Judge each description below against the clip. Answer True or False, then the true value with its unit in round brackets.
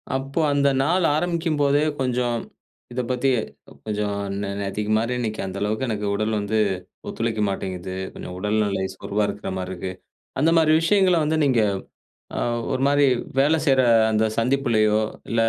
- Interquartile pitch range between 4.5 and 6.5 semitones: True (5.2 semitones)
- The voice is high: False (115 Hz)